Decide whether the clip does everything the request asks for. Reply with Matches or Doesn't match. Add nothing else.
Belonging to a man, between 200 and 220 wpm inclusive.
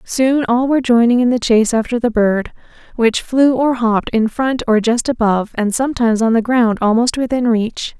Doesn't match